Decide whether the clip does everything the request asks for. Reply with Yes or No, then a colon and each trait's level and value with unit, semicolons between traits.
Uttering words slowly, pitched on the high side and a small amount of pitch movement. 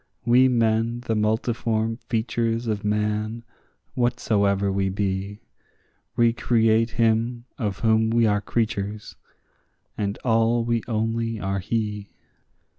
No: slow, 110 wpm; low, 110 Hz; narrow, 1.9 semitones